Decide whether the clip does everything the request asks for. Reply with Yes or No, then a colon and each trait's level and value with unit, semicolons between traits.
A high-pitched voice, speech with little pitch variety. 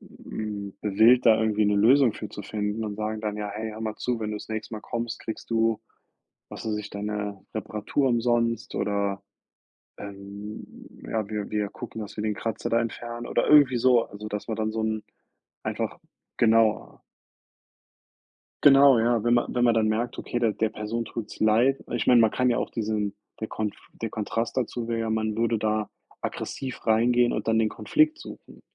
No: low, 110 Hz; narrow, 1.8 semitones